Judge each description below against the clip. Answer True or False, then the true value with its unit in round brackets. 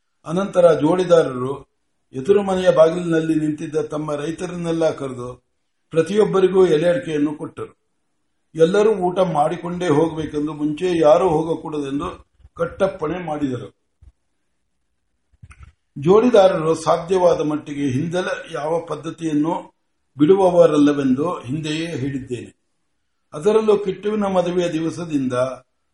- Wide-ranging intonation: False (3.4 semitones)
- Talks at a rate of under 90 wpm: True (80 wpm)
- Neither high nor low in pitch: True (160 Hz)